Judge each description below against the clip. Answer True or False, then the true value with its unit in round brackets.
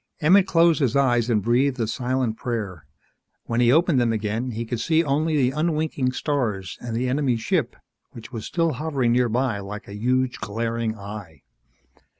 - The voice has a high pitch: False (125 Hz)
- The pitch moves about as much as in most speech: True (3.9 semitones)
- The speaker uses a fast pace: False (170 wpm)